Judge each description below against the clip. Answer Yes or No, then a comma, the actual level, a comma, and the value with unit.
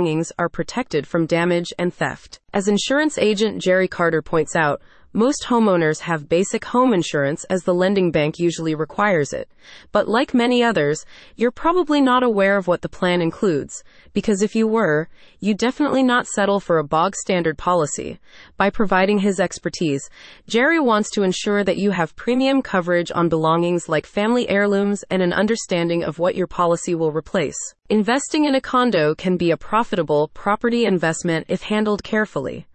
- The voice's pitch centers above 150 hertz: Yes, medium, 185 Hz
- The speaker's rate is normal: Yes, average, 170 wpm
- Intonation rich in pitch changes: No, average, 4.8 semitones